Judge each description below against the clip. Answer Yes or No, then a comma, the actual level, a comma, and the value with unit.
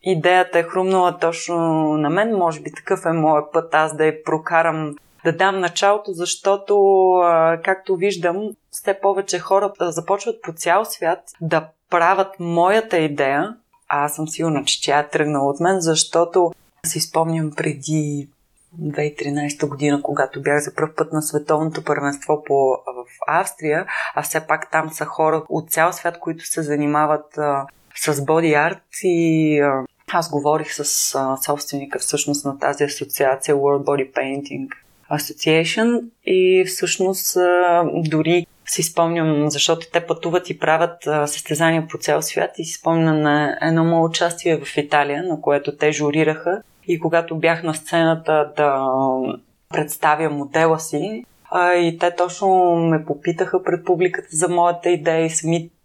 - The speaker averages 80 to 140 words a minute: No, average, 150 wpm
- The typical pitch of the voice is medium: Yes, medium, 160 Hz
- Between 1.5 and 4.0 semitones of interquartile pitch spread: Yes, average, 2.8 semitones